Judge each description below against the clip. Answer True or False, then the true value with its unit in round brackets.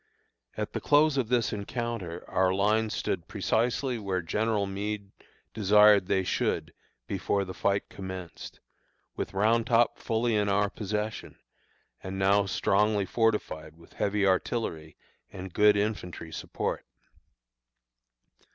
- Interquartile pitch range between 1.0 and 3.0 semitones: True (2.6 semitones)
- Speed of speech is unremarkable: False (125 wpm)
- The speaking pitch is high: False (105 Hz)